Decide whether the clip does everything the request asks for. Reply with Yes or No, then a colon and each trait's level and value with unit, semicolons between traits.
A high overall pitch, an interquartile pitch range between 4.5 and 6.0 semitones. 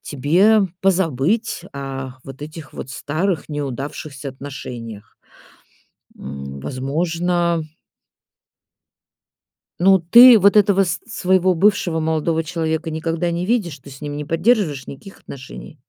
No: medium, 160 Hz; average, 5.0 semitones